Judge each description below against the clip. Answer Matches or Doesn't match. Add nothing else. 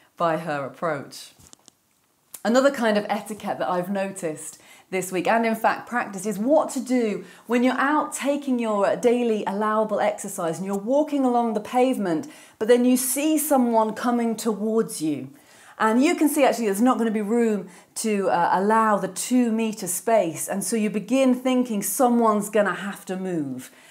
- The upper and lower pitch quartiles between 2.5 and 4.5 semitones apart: Matches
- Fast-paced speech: Doesn't match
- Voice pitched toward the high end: Matches